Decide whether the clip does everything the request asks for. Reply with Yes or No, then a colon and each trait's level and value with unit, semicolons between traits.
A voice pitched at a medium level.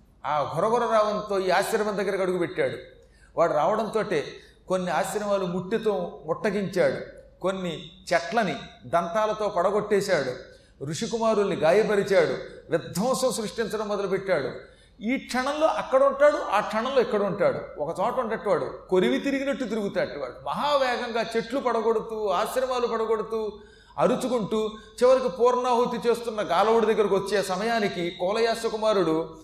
No: high, 220 Hz